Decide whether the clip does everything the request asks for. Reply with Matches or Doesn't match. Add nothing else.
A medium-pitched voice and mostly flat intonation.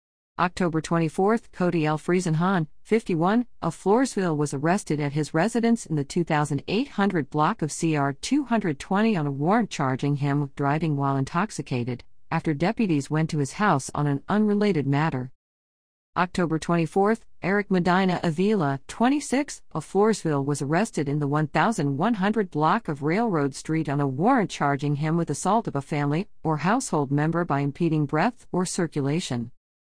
Doesn't match